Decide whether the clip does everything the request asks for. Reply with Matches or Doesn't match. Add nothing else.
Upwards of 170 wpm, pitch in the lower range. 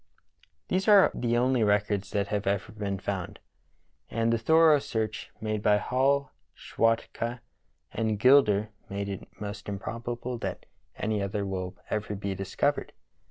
Doesn't match